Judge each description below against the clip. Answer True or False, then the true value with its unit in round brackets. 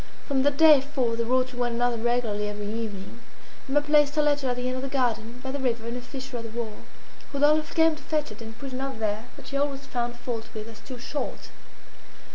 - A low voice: False (250 Hz)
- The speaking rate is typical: False (240 wpm)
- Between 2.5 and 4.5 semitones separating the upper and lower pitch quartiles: True (3.4 semitones)